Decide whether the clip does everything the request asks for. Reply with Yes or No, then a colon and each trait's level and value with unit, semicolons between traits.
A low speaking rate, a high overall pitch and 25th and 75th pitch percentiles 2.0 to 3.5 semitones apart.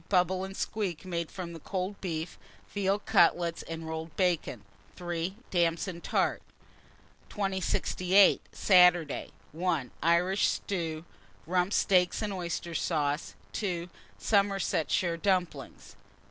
No: slow, 105 wpm; medium, 180 Hz; narrow, 2.4 semitones